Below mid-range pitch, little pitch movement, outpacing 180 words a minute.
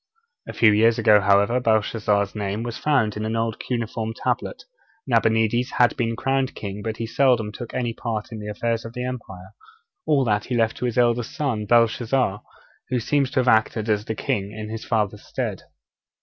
Yes: low, 115 Hz; narrow, 2.3 semitones; average, 190 wpm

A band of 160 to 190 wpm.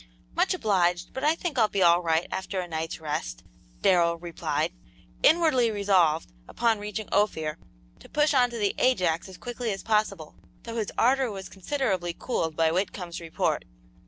Yes: average, 165 wpm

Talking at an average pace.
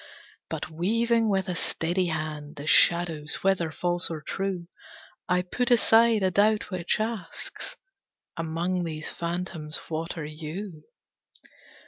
No: slow, 125 wpm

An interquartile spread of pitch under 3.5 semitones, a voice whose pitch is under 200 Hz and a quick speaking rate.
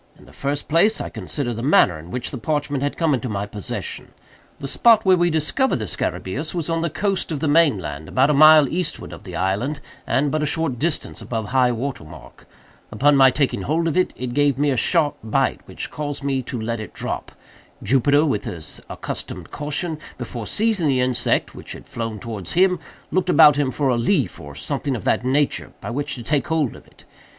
No: average, 4.7 semitones; medium, 140 Hz; fast, 215 wpm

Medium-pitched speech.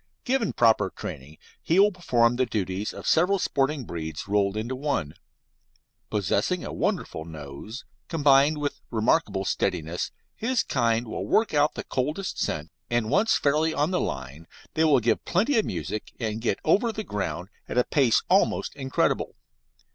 No: low, 120 Hz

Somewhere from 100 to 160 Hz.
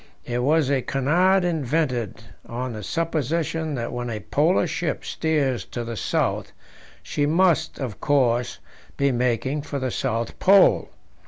Yes: medium, 140 Hz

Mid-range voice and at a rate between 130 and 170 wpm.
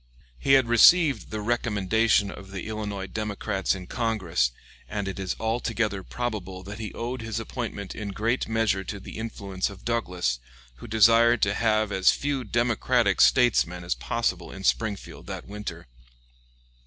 No: low, 110 Hz; average, 155 wpm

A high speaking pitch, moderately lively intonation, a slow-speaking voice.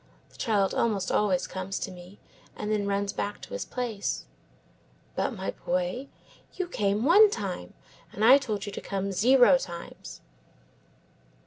No: high, 205 Hz; average, 4.3 semitones; average, 150 wpm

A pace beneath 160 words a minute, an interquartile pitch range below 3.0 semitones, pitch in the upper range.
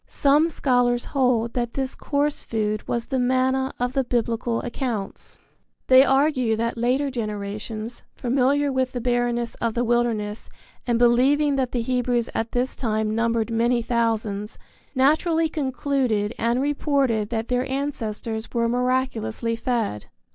Yes: average, 140 wpm; narrow, 2.5 semitones; high, 245 Hz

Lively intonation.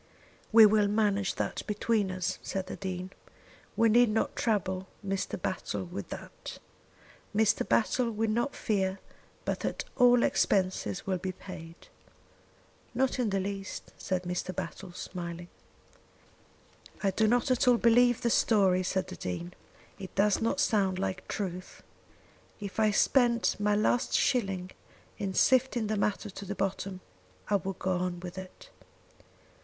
No: average, 3.1 semitones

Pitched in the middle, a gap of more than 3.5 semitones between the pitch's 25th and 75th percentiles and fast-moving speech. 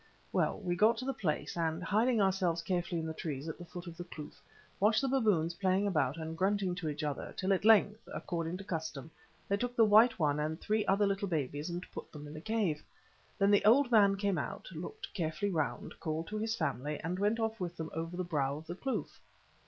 Yes: medium, 180 Hz; average, 4.5 semitones; fast, 230 wpm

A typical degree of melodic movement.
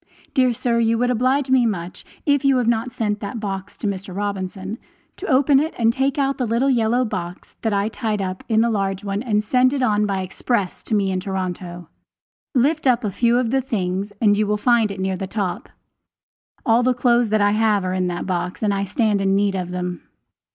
Yes: average, 4.1 semitones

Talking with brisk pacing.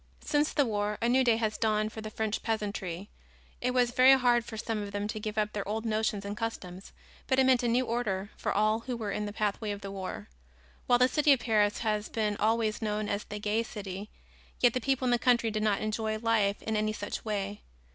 Yes: fast, 235 wpm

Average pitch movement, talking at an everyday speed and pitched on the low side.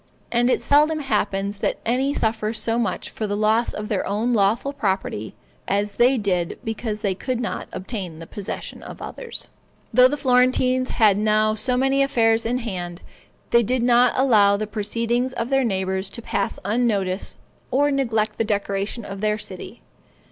No: average, 3.7 semitones; average, 170 wpm; high, 225 Hz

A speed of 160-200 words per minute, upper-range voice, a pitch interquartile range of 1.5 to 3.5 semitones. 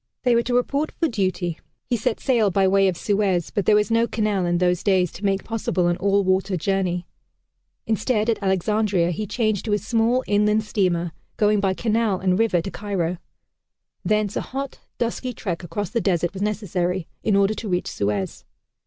Yes: average, 190 wpm; high, 200 Hz; average, 3.2 semitones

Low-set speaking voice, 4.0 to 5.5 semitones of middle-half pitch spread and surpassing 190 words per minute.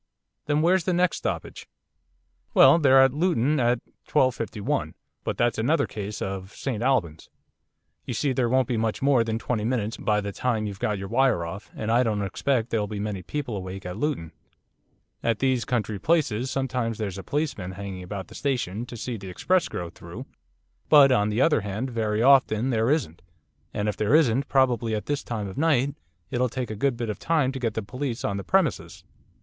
Yes: low, 115 Hz; average, 4.3 semitones; average, 200 wpm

